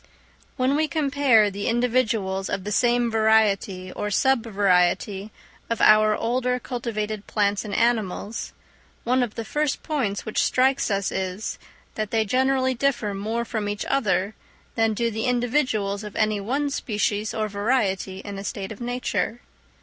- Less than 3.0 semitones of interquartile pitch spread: No, average, 3.5 semitones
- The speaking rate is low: No, average, 155 wpm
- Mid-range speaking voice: No, high, 220 Hz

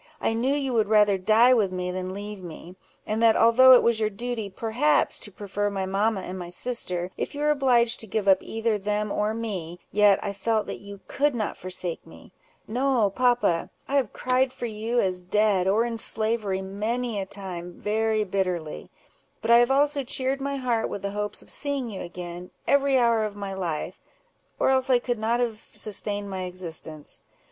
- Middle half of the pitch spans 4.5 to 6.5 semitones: No, average, 3.9 semitones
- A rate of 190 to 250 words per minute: Yes, average, 200 wpm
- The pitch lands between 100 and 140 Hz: No, high, 215 Hz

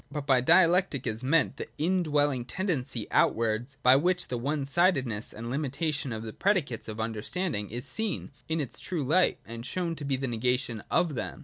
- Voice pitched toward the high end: No, medium, 140 Hz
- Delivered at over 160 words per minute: Yes, average, 190 wpm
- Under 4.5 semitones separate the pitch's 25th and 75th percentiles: No, wide, 5.5 semitones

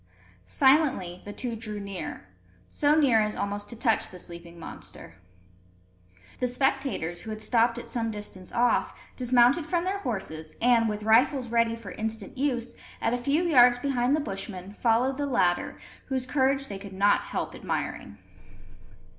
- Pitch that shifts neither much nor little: Yes, average, 4.5 semitones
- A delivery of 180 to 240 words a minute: No, average, 160 wpm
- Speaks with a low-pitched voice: No, high, 230 Hz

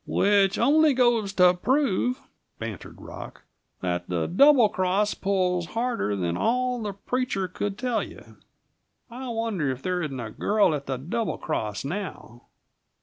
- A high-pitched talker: Yes, high, 195 Hz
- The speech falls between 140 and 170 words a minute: Yes, average, 145 wpm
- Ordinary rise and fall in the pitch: No, wide, 8.7 semitones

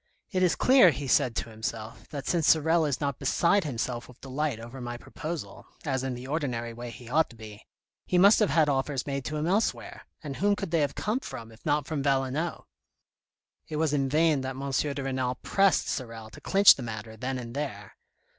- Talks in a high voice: No, medium, 140 Hz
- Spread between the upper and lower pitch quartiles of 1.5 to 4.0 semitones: No, average, 4.5 semitones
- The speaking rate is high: Yes, fast, 210 wpm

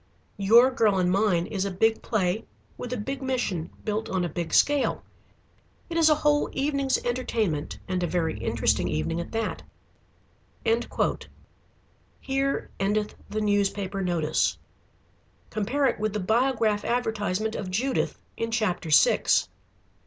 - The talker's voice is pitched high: Yes, high, 215 Hz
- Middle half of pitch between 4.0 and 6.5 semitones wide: Yes, average, 5.2 semitones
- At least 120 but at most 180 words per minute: Yes, average, 140 wpm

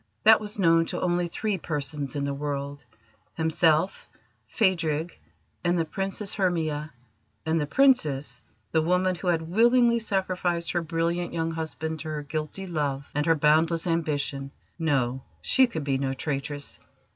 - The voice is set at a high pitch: No, medium, 160 Hz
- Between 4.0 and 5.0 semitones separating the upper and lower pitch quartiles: No, average, 3.3 semitones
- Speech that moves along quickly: No, average, 150 wpm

